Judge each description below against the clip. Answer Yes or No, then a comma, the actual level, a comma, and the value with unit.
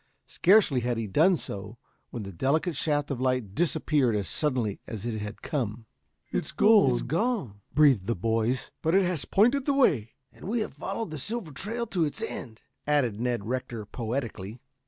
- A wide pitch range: Yes, wide, 7.1 semitones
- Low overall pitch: Yes, low, 130 Hz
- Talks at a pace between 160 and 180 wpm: Yes, average, 175 wpm